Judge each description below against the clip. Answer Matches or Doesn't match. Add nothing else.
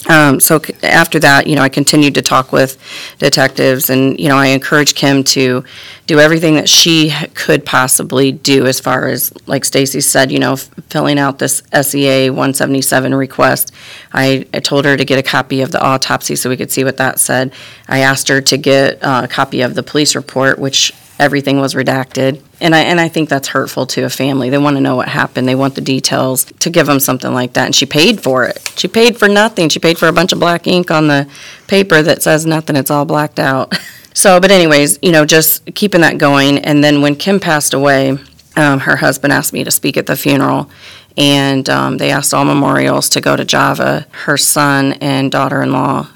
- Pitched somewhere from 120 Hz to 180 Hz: Matches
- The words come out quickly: Matches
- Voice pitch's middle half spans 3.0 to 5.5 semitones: Doesn't match